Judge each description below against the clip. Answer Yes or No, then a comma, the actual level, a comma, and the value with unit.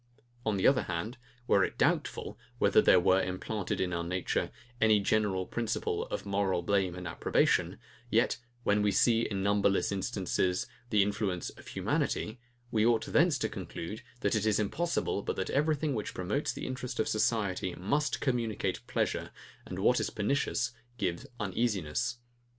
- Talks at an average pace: Yes, average, 160 wpm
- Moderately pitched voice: No, low, 105 Hz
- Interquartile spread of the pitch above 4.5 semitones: No, average, 3.6 semitones